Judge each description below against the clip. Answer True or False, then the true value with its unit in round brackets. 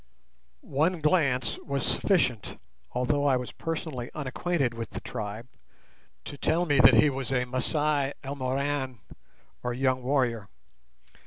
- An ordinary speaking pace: False (115 wpm)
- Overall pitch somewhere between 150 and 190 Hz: False (135 Hz)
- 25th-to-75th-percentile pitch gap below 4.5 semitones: True (2.9 semitones)